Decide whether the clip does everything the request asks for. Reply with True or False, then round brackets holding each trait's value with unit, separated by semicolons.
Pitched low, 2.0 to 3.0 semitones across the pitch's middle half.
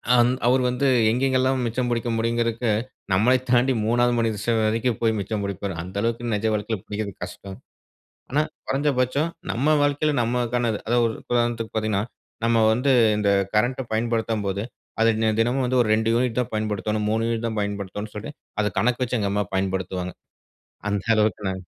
True (115 Hz; 2.7 semitones)